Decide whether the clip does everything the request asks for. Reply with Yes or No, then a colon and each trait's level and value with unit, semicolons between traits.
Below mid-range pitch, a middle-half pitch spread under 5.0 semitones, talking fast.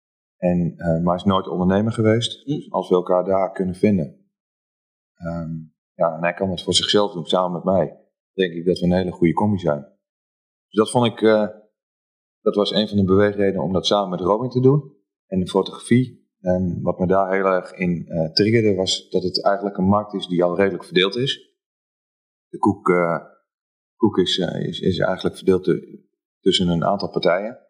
Yes: very low, 95 Hz; average, 3.0 semitones; fast, 205 wpm